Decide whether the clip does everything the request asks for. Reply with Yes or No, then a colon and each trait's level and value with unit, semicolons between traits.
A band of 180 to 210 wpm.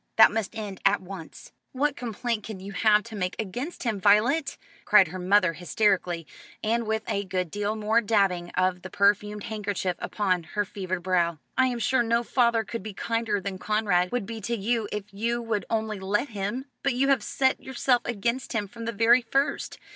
Yes: average, 195 wpm